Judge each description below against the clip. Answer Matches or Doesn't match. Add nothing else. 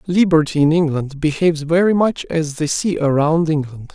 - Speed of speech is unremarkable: Matches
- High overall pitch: Doesn't match